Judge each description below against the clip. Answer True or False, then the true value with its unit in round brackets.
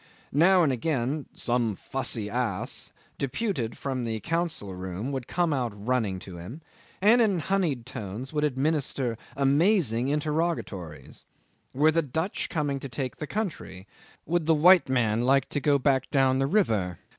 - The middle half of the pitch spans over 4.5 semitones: True (5.2 semitones)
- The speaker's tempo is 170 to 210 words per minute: False (155 wpm)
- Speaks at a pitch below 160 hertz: True (135 Hz)